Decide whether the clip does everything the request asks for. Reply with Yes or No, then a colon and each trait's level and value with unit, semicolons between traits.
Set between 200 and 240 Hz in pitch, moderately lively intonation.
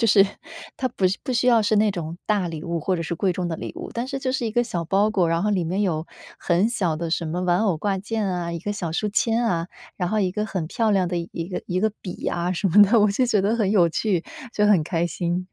No: high, 190 Hz; average, 3.8 semitones